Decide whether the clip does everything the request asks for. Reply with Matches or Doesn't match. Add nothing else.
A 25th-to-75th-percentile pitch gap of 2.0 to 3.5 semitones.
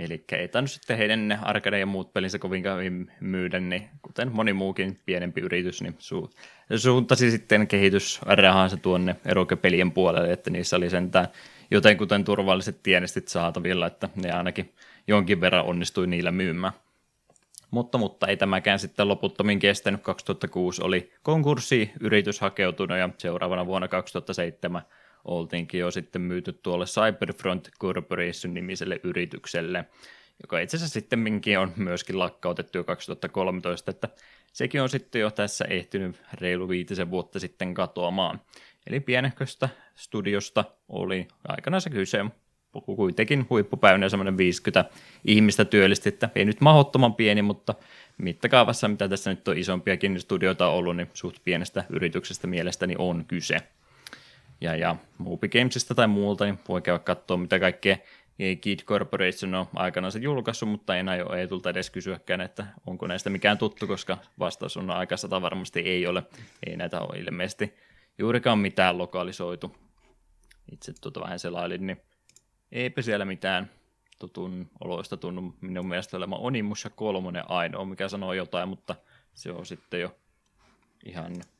Matches